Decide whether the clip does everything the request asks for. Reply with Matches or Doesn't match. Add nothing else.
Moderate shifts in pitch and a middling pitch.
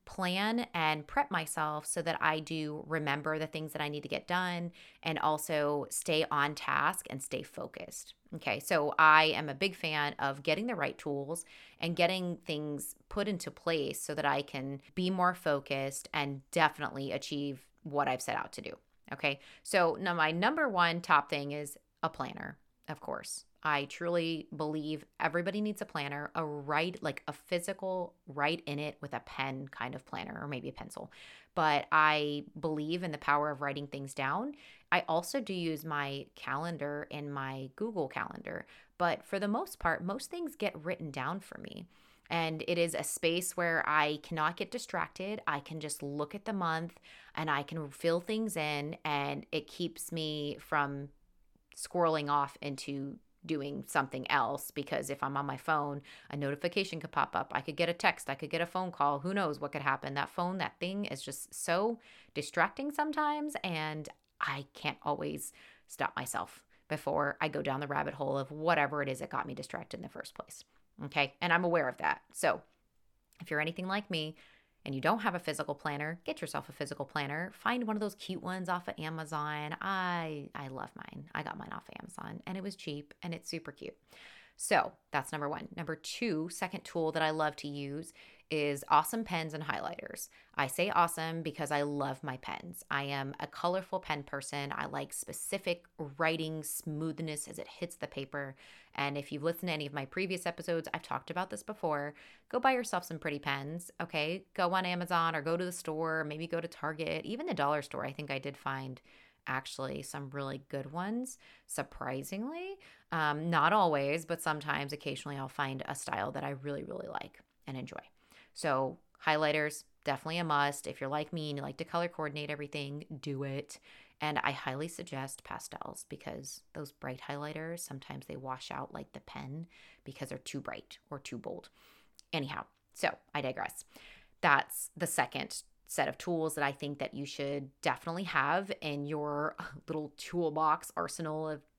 Matches